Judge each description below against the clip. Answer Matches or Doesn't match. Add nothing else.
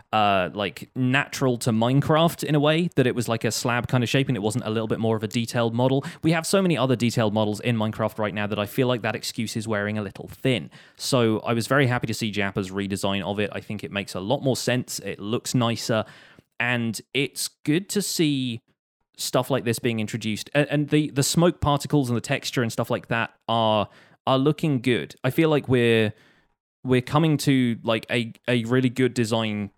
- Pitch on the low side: Matches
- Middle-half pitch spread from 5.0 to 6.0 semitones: Doesn't match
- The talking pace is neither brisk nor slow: Doesn't match